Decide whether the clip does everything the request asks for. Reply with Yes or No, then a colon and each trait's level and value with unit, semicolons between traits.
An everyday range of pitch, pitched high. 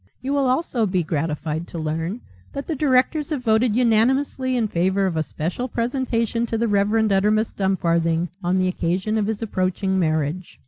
No: wide, 5.7 semitones; high, 210 Hz